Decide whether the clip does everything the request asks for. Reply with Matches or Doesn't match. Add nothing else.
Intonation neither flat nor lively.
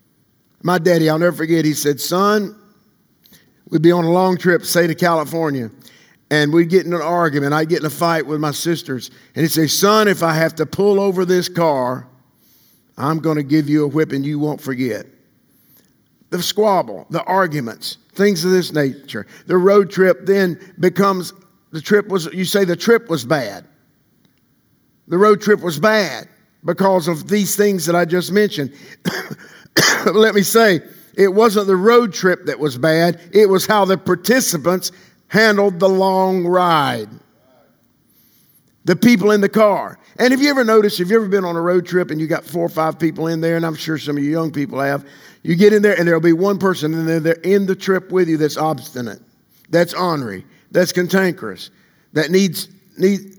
Matches